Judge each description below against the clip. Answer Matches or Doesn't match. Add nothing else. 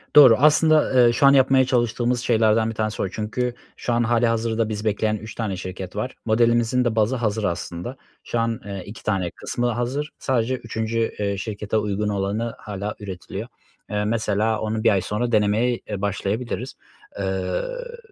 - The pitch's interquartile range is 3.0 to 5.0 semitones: Doesn't match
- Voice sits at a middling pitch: Doesn't match